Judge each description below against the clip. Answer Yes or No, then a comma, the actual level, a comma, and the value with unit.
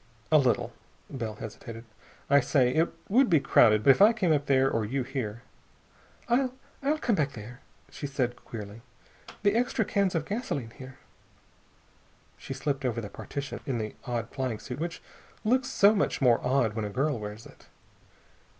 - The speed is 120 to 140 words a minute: No, average, 175 wpm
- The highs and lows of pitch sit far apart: Yes, wide, 6.2 semitones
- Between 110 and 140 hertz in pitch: Yes, low, 135 Hz